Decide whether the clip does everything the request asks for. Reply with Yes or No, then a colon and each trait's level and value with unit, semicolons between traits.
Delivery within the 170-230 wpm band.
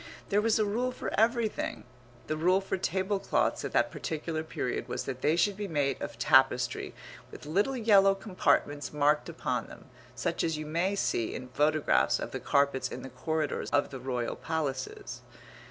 Yes: average, 175 wpm